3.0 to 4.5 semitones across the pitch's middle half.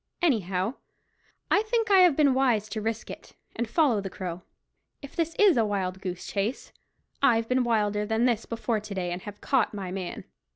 No: average, 5.1 semitones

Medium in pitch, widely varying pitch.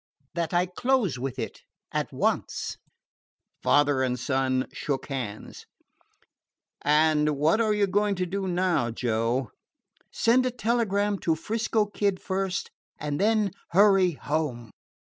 Yes: medium, 175 Hz; wide, 7.0 semitones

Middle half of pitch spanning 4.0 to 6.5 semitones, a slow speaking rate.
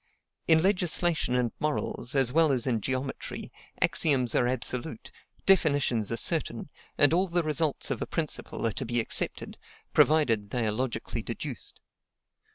No: average, 4.9 semitones; average, 150 wpm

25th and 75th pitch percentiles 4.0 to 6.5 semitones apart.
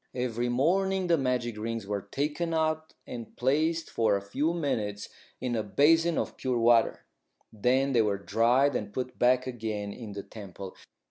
Yes: average, 5.2 semitones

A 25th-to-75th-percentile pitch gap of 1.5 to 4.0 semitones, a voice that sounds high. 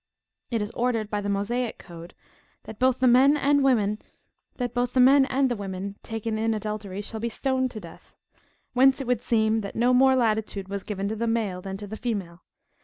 Yes: average, 3.6 semitones; high, 225 Hz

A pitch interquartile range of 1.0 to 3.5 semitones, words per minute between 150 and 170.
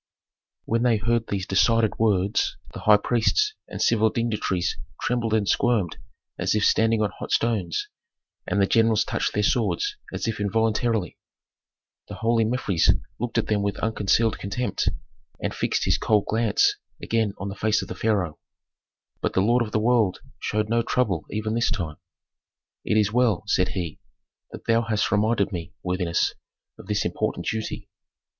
Yes: narrow, 2.4 semitones; average, 165 wpm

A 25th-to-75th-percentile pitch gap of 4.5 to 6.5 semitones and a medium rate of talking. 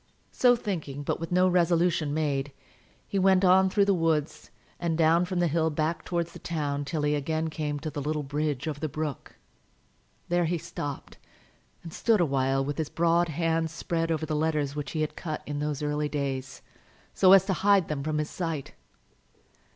No: average, 2.7 semitones; average, 195 wpm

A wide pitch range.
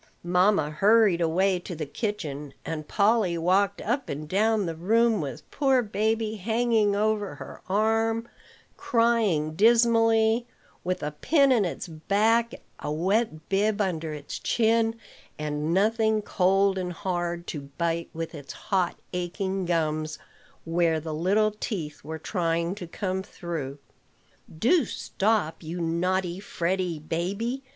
No: average, 5.0 semitones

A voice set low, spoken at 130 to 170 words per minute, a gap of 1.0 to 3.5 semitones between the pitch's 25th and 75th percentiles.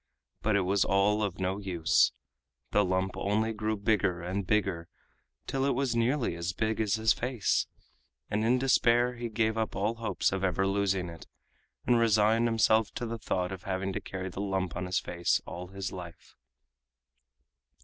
No: low, 100 Hz; average, 180 wpm; average, 3.1 semitones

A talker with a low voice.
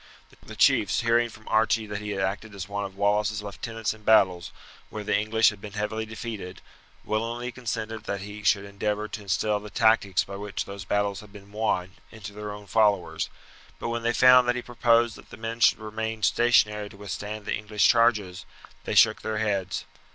Yes: low, 105 Hz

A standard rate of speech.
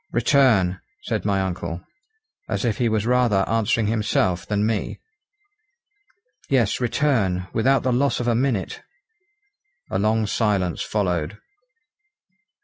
No: slow, 120 wpm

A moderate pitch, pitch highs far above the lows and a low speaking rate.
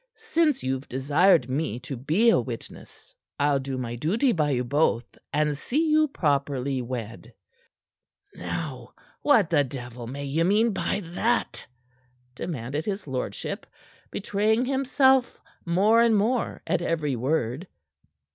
Yes: medium, 150 Hz; wide, 8.9 semitones; slow, 130 wpm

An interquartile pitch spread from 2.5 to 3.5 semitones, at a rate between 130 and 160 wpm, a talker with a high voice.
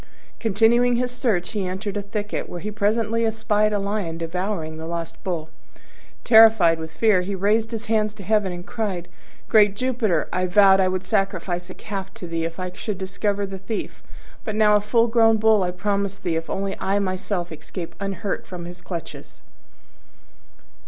No: average, 3.1 semitones; average, 180 wpm; high, 200 Hz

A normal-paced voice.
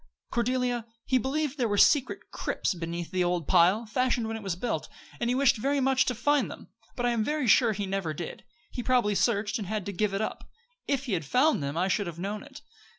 No: fast, 240 wpm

